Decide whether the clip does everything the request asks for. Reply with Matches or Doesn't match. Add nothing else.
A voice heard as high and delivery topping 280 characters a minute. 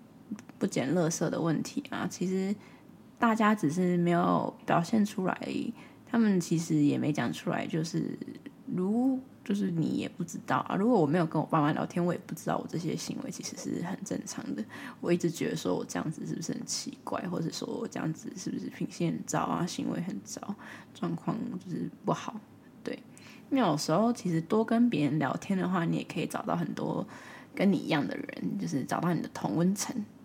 Matches